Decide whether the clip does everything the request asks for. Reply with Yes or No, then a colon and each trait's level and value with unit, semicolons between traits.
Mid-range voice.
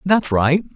Yes: medium, 160 Hz